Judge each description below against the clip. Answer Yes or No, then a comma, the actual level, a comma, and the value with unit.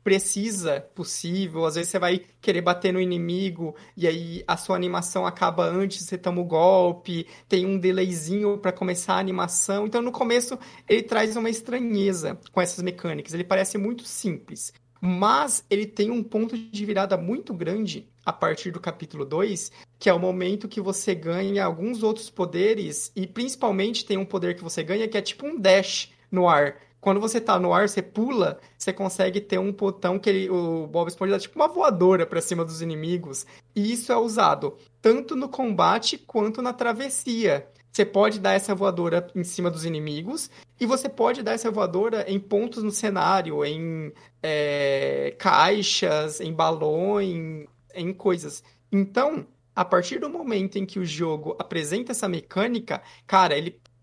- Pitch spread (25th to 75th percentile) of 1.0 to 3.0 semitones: No, average, 3.7 semitones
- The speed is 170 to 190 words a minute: Yes, average, 175 wpm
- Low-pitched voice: No, high, 190 Hz